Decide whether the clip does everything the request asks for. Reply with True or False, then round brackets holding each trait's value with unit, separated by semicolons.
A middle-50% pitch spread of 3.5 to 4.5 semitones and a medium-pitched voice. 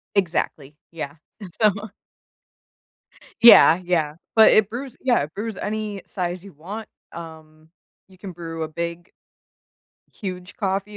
True (4.2 semitones; 180 Hz)